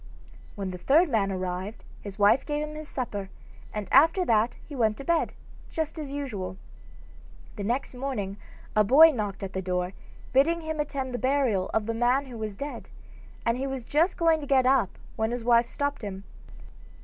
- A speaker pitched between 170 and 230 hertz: No, high, 245 Hz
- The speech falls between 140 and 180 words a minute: No, average, 190 wpm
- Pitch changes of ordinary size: No, wide, 5.8 semitones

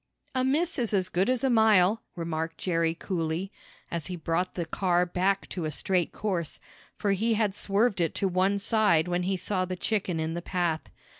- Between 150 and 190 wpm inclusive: No, average, 200 wpm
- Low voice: No, medium, 185 Hz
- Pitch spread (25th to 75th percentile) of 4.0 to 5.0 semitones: No, average, 3.3 semitones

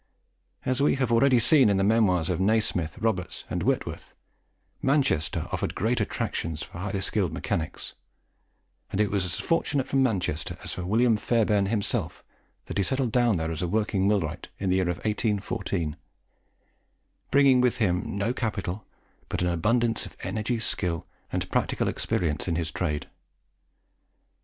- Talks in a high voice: No, low, 100 Hz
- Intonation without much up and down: No, average, 4.7 semitones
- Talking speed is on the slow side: No, average, 155 wpm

